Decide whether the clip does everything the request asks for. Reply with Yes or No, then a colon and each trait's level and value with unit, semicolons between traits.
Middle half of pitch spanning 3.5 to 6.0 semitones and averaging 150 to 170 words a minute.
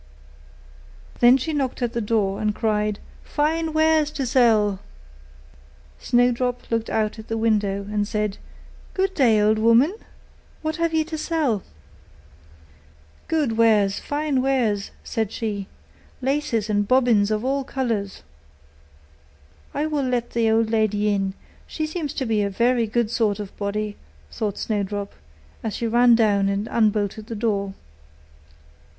No: average, 3.8 semitones; average, 140 wpm